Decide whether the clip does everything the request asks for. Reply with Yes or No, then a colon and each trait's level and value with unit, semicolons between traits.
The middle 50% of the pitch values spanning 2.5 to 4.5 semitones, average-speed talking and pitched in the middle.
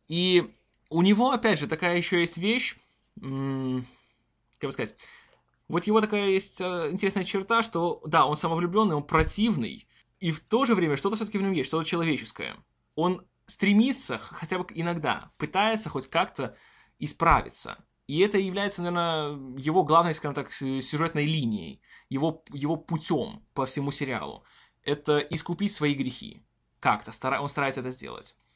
No: average, 5.2 semitones; average, 150 wpm; medium, 165 Hz